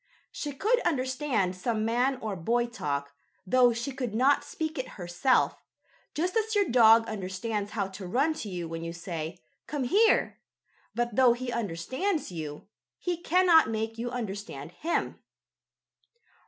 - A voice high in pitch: Yes, high, 235 Hz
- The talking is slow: No, average, 150 wpm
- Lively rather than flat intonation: Yes, wide, 6.7 semitones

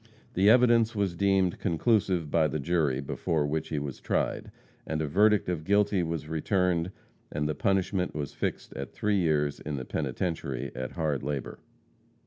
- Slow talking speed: No, average, 165 wpm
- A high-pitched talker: No, very low, 80 Hz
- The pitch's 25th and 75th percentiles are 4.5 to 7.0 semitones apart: Yes, average, 4.8 semitones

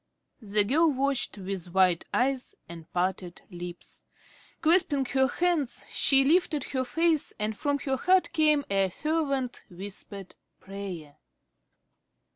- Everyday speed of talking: No, slow, 120 wpm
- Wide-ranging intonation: Yes, wide, 7.5 semitones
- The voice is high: Yes, very high, 255 Hz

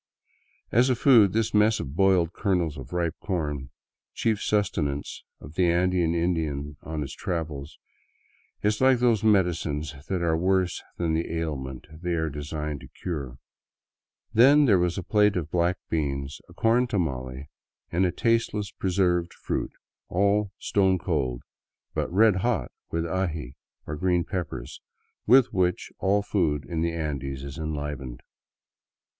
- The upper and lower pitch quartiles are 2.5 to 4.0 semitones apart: No, average, 4.7 semitones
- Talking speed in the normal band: Yes, average, 150 wpm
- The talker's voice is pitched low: Yes, very low, 85 Hz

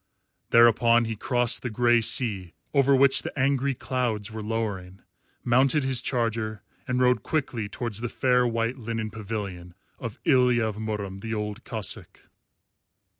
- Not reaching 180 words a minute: Yes, average, 145 wpm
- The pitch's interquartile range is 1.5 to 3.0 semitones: Yes, average, 2.7 semitones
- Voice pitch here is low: Yes, low, 115 Hz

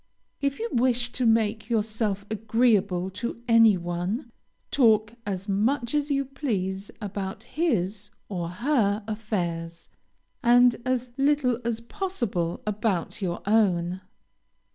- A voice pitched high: Yes, high, 220 Hz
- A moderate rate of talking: No, slow, 120 wpm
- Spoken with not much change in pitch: No, average, 4.2 semitones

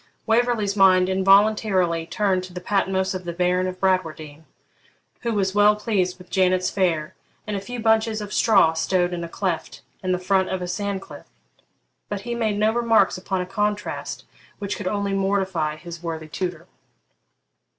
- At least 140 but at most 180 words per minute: Yes, average, 170 wpm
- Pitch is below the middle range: No, high, 190 Hz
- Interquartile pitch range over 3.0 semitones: No, narrow, 2.4 semitones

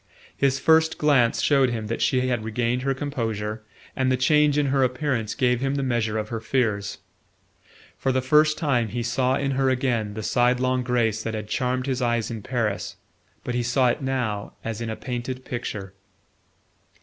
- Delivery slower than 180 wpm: No, average, 185 wpm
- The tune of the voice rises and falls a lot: No, average, 2.8 semitones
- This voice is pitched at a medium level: No, low, 125 Hz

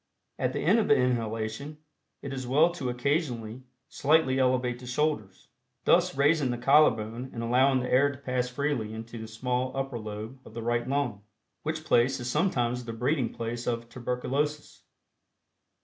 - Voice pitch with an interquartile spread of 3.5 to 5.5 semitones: No, average, 3.1 semitones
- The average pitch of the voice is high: No, low, 125 Hz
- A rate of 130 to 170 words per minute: Yes, average, 165 wpm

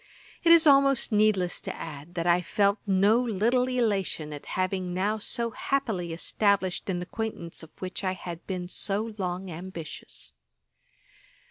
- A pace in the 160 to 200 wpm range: No, average, 145 wpm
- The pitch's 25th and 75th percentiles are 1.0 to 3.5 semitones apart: No, average, 3.9 semitones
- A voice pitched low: No, high, 190 Hz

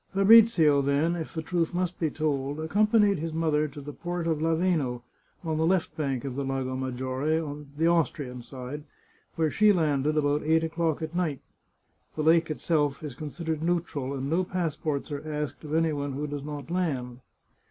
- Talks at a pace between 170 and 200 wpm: Yes, average, 185 wpm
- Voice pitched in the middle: Yes, medium, 155 Hz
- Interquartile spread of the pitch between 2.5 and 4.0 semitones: Yes, average, 2.8 semitones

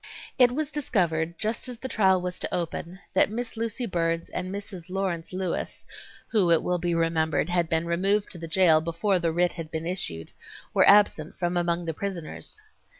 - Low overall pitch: No, medium, 175 Hz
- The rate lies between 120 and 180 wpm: No, average, 190 wpm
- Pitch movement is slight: No, average, 3.2 semitones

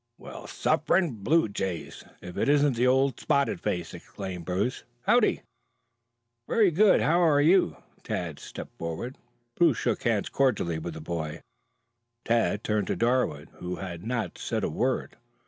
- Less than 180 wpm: Yes, average, 145 wpm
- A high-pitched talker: No, low, 110 Hz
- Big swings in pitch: Yes, wide, 7.9 semitones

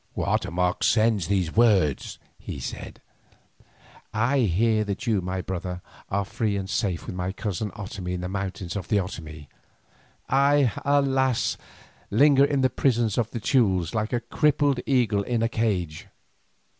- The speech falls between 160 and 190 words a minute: No, average, 150 wpm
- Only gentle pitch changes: No, average, 4.7 semitones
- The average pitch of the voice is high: No, low, 105 Hz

